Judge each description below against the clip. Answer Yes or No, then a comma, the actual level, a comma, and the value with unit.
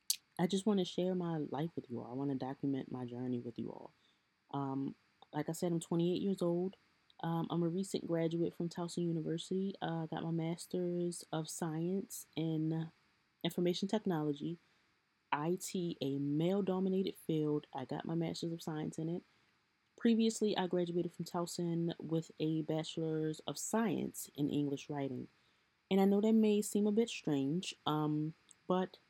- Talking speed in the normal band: Yes, average, 165 wpm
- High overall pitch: No, medium, 165 Hz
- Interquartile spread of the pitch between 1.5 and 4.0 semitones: Yes, average, 3.2 semitones